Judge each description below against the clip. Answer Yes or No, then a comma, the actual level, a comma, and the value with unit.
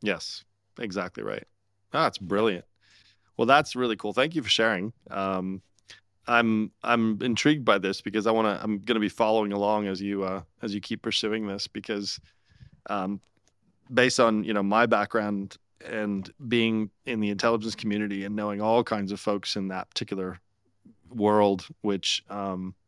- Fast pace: No, average, 160 wpm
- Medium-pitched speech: No, low, 105 Hz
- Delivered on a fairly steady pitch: Yes, narrow, 2.2 semitones